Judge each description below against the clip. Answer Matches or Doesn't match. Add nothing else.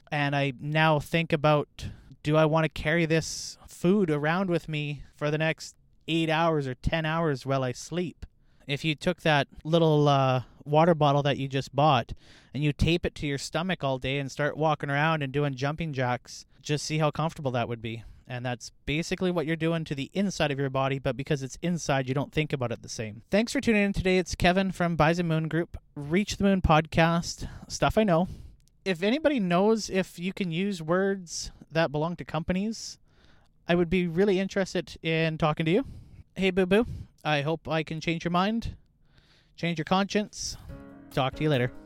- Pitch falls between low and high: Matches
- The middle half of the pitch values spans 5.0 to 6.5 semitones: Doesn't match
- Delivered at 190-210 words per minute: Matches